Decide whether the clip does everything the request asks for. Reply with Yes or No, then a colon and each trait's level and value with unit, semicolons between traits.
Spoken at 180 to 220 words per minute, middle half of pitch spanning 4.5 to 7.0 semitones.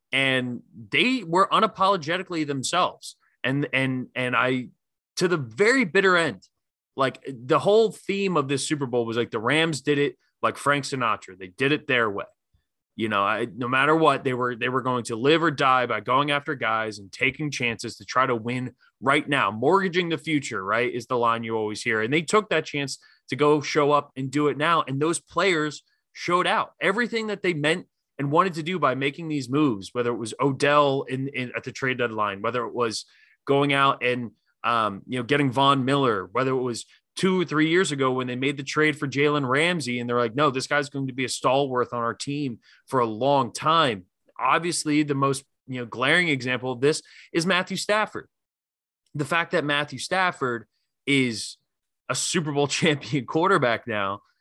No: fast, 205 wpm; average, 3.9 semitones